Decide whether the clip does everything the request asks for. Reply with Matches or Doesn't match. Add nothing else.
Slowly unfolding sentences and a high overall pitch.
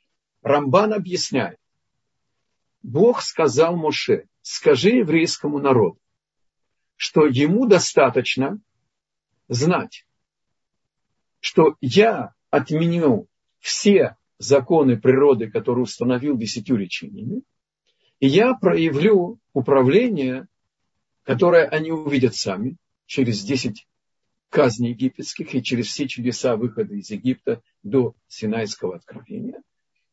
Doesn't match